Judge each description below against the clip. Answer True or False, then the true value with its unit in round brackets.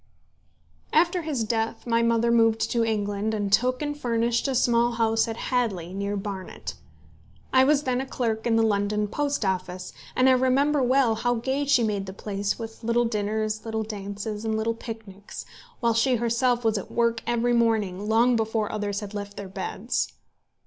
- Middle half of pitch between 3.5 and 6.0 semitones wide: False (2.6 semitones)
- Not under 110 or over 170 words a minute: False (180 wpm)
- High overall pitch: True (225 Hz)